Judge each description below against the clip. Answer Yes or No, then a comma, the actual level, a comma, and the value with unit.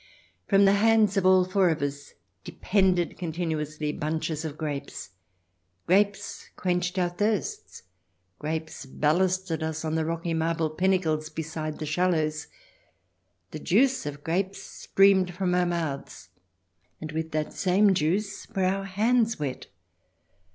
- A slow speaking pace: Yes, slow, 130 wpm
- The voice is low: No, medium, 170 Hz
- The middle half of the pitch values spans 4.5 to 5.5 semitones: No, average, 3.5 semitones